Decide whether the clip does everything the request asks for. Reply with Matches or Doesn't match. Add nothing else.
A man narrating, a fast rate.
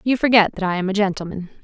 Doesn't match